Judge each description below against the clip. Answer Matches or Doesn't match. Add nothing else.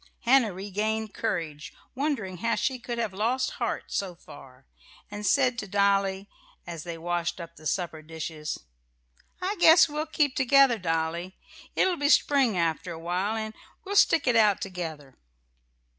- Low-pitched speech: Doesn't match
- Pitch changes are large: Matches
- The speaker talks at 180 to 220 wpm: Doesn't match